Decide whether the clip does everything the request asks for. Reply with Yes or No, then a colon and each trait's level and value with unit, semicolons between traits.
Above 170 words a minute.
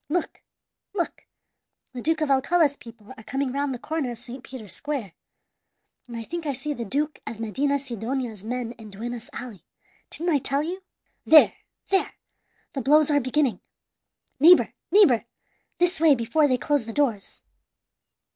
No: average, 155 wpm